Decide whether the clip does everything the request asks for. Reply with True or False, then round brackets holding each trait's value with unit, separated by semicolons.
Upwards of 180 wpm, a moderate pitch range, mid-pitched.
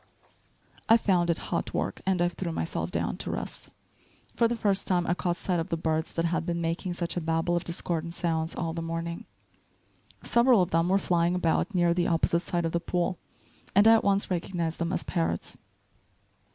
False (205 wpm; 1.6 semitones; 175 Hz)